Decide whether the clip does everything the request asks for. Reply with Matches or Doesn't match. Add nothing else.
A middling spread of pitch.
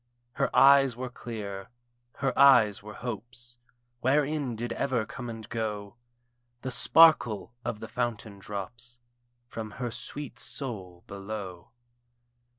Matches